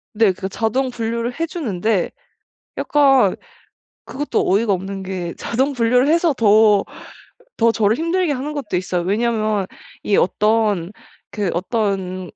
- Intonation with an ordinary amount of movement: Yes, average, 4.6 semitones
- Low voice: No, high, 220 Hz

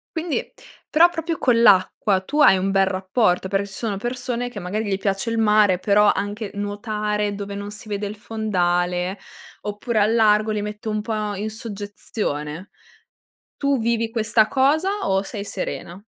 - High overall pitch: Yes, high, 210 Hz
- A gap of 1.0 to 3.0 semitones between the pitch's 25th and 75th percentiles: Yes, narrow, 2.5 semitones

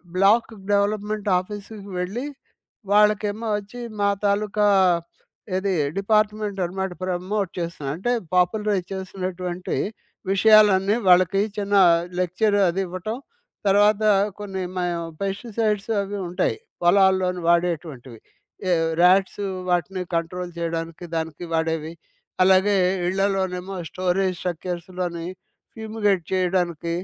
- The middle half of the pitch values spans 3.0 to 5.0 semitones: No, narrow, 2.5 semitones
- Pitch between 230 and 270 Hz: No, high, 190 Hz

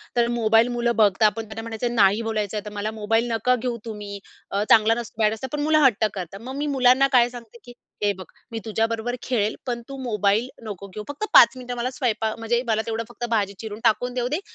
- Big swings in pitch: No, narrow, 2.4 semitones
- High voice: Yes, high, 225 Hz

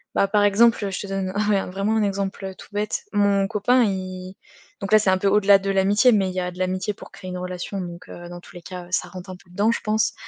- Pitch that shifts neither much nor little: No, narrow, 1.9 semitones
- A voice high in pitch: Yes, high, 195 Hz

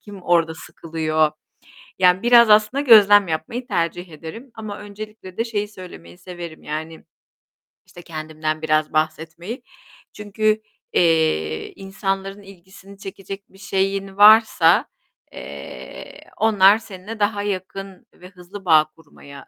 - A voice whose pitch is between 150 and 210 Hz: Yes, high, 190 Hz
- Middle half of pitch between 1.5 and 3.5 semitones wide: No, average, 4.2 semitones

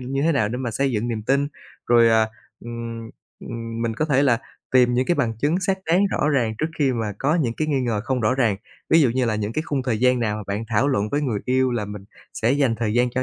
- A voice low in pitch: Yes, low, 125 Hz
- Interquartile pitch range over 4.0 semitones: No, average, 3.4 semitones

